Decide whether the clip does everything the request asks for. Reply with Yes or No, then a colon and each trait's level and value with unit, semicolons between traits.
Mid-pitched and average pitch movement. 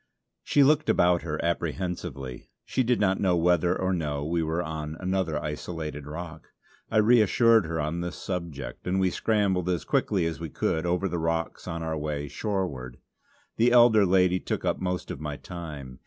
No: very low, 85 Hz; average, 3.3 semitones